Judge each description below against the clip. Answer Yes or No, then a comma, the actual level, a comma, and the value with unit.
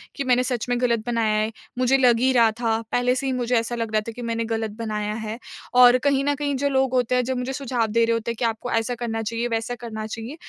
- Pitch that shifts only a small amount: Yes, narrow, 1.9 semitones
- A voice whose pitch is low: No, high, 240 Hz